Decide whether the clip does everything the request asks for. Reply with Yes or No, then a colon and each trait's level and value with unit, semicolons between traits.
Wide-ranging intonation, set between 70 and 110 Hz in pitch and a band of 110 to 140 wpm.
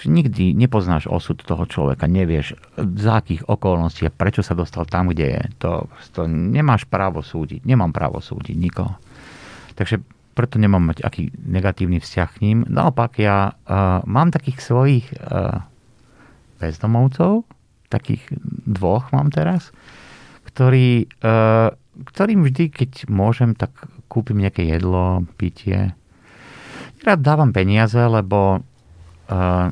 Yes: wide, 6.1 semitones; low, 105 Hz; average, 125 wpm